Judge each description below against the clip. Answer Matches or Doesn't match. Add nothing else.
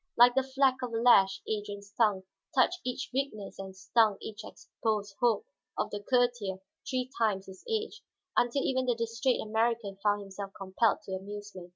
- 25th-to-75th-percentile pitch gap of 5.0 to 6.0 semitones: Doesn't match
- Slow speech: Doesn't match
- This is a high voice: Matches